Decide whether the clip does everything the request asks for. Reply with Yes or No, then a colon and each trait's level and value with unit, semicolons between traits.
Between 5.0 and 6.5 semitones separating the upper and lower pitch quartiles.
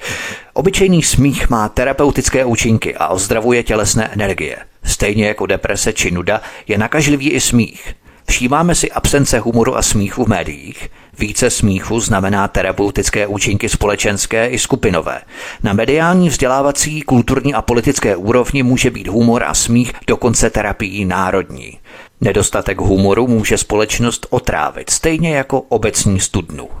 No: average, 4.1 semitones